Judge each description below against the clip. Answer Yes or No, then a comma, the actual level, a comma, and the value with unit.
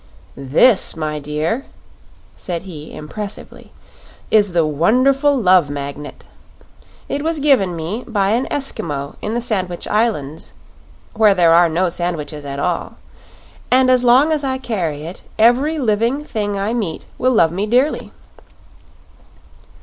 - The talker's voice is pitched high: Yes, high, 200 Hz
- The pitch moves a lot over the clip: Yes, wide, 7.2 semitones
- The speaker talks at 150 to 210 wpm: No, slow, 135 wpm